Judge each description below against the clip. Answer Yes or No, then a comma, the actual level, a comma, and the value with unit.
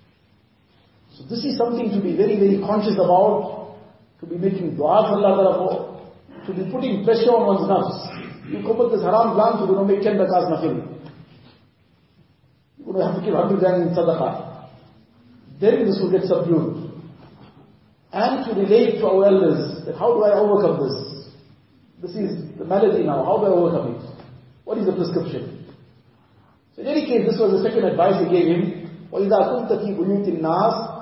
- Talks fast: No, average, 160 wpm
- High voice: No, medium, 180 Hz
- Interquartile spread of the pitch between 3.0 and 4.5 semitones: No, wide, 5.4 semitones